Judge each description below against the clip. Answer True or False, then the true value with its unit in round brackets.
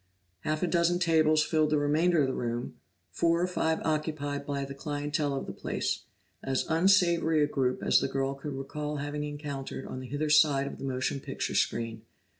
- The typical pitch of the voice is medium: True (145 Hz)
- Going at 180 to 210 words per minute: True (195 wpm)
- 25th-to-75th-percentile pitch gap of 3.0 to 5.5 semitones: False (2.5 semitones)